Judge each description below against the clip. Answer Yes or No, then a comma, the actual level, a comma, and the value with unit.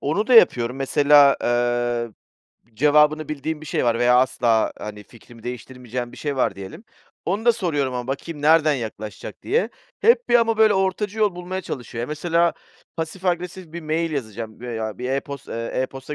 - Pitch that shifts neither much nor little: No, wide, 6.0 semitones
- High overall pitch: No, medium, 140 Hz